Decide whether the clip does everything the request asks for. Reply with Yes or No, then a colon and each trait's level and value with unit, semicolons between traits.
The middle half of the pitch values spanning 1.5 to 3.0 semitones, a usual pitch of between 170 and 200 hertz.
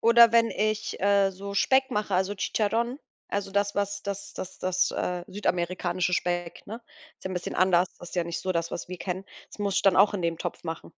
Yes: narrow, 2.5 semitones; high, 190 Hz